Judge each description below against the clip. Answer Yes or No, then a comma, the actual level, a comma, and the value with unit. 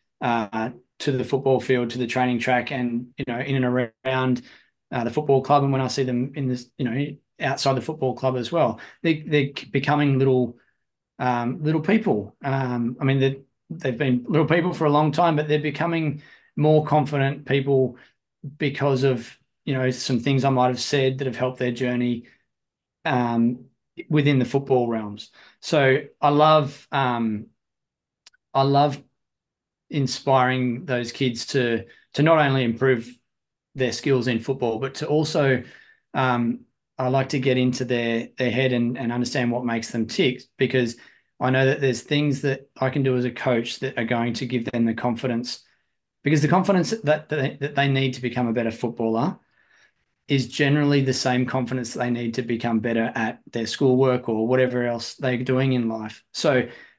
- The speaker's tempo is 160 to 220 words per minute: Yes, average, 180 wpm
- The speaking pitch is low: Yes, low, 130 Hz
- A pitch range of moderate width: No, narrow, 2.3 semitones